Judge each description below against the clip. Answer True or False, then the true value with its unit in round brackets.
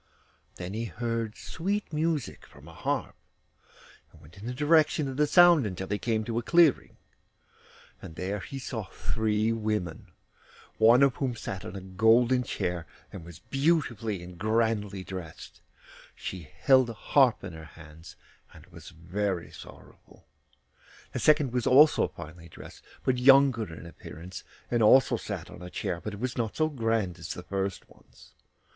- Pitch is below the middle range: True (110 Hz)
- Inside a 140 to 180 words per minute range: True (165 wpm)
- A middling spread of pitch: False (5.9 semitones)